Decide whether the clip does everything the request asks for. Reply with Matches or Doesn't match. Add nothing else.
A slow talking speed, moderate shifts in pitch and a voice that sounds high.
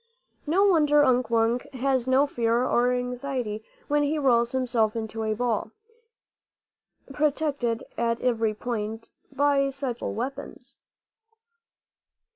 Matches